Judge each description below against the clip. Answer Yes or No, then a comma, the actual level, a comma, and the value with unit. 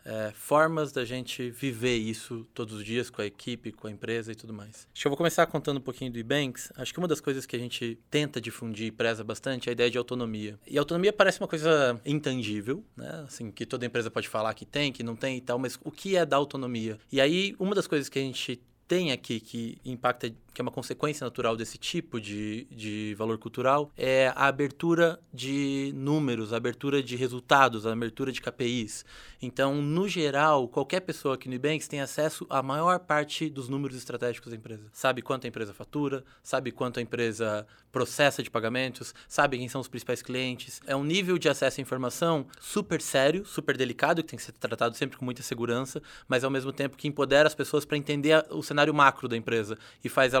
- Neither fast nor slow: No, fast, 215 wpm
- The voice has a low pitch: Yes, low, 130 Hz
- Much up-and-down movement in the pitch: No, average, 3.5 semitones